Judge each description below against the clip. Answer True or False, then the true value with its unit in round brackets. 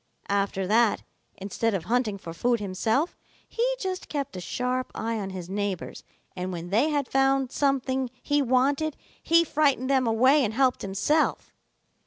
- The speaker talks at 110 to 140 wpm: False (160 wpm)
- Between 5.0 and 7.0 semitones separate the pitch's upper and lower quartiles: True (5.6 semitones)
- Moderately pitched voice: False (250 Hz)